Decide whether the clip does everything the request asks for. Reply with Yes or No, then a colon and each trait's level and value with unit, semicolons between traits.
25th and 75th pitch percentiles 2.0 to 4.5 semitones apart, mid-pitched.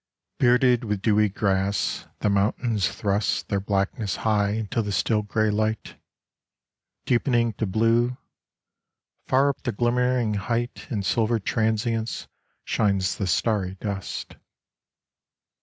No: average, 2.7 semitones; low, 110 Hz